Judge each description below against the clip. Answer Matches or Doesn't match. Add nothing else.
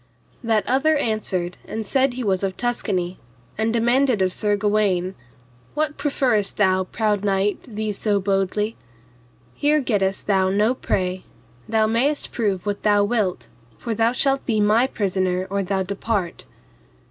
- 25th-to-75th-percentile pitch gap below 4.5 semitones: Matches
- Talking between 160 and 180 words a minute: Doesn't match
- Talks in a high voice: Matches